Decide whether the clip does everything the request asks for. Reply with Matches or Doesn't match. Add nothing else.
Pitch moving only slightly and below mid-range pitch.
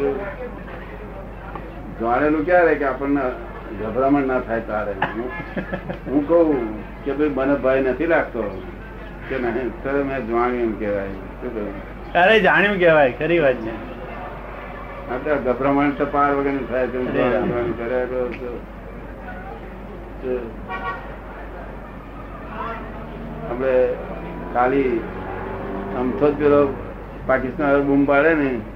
Doesn't match